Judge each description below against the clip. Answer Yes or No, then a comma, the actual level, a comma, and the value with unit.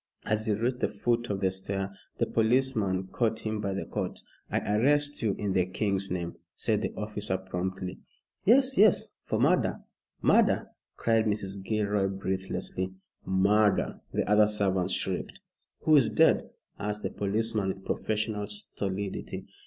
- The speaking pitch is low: Yes, low, 105 Hz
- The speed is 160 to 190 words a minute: No, average, 150 wpm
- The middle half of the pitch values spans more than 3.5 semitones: No, narrow, 2.4 semitones